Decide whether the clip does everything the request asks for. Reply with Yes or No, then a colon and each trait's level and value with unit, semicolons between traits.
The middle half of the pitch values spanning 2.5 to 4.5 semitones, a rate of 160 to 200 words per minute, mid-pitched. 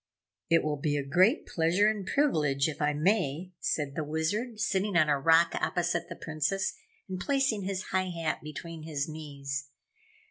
Yes: average, 4.2 semitones; average, 170 wpm; medium, 165 Hz